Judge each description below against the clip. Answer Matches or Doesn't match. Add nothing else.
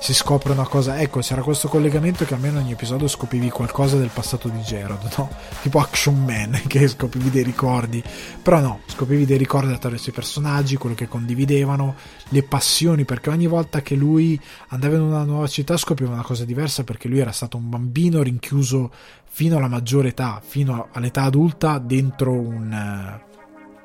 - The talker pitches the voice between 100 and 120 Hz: Doesn't match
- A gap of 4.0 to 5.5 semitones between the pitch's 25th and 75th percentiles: Doesn't match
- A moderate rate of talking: Doesn't match